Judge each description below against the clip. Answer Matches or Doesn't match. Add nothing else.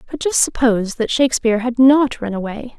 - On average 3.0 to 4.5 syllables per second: Doesn't match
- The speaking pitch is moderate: Doesn't match